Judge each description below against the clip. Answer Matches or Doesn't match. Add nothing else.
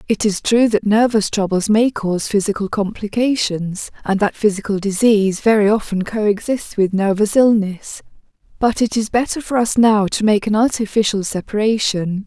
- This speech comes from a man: Doesn't match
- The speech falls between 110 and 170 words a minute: Matches